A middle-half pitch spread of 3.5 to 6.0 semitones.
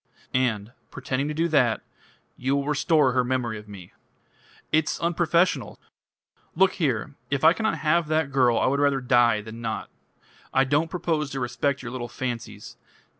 Yes: average, 4.2 semitones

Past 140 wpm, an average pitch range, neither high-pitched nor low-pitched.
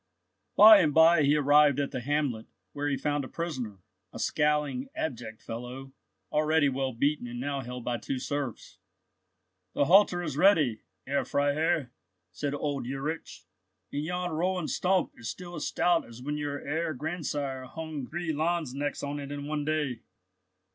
Yes: average, 160 wpm; average, 3.0 semitones; medium, 145 Hz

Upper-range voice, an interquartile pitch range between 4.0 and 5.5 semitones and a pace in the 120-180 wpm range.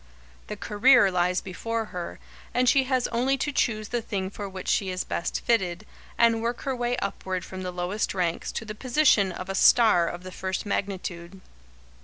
No: high, 200 Hz; average, 4.3 semitones; average, 190 wpm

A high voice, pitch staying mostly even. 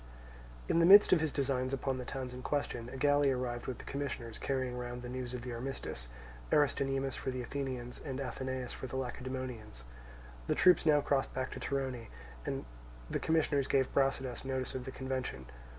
No: low, 130 Hz; narrow, 1.7 semitones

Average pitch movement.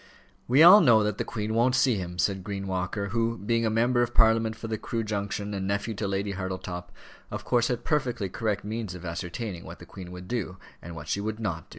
Yes: average, 3.4 semitones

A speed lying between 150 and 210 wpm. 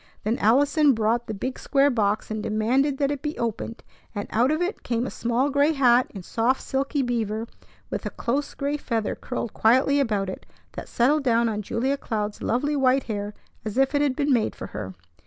Yes: fast, 205 wpm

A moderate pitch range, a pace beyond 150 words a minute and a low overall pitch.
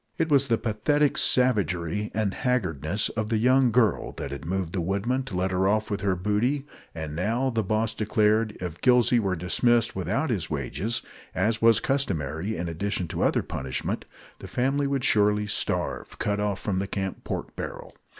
Yes: average, 4.3 semitones; average, 180 wpm; low, 105 Hz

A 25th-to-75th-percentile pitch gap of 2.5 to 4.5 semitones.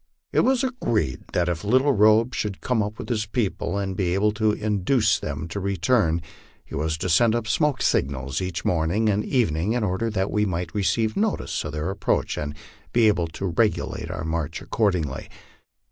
No: average, 4.9 semitones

